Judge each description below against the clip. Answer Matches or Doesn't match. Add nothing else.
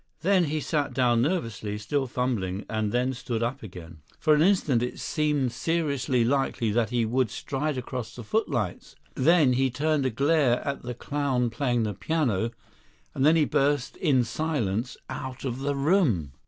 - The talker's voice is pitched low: Matches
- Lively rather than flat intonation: Doesn't match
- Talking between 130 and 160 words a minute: Doesn't match